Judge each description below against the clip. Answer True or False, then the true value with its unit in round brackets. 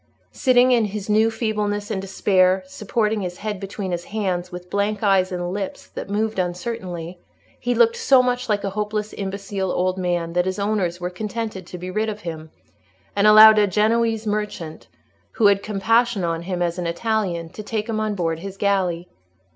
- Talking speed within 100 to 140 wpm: False (185 wpm)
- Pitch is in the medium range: False (200 Hz)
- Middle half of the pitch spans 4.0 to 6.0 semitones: False (3.0 semitones)